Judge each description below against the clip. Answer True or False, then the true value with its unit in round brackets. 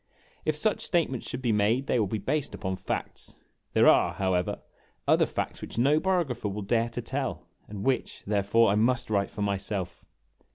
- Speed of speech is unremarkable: True (180 wpm)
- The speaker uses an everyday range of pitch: True (4.6 semitones)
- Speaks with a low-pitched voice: True (110 Hz)